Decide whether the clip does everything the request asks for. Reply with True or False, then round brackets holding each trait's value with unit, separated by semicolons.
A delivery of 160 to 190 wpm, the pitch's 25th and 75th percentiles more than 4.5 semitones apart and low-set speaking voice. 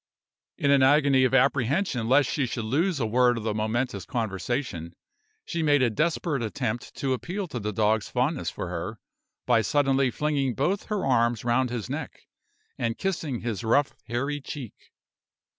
False (165 wpm; 4.0 semitones; 125 Hz)